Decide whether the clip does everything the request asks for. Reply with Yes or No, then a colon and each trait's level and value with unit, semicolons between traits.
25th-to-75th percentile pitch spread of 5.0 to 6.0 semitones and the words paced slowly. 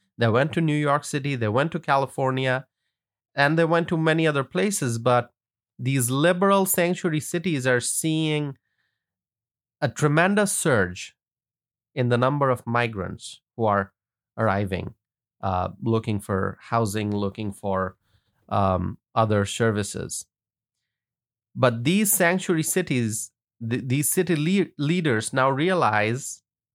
Yes: wide, 5.5 semitones; slow, 125 wpm